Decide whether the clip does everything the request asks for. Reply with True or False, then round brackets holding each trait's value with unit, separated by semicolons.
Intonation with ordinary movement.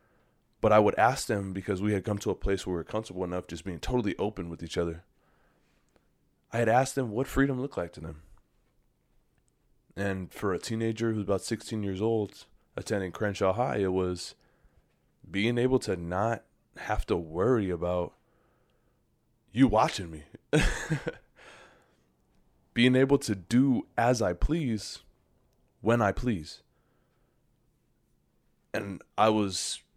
True (4.7 semitones)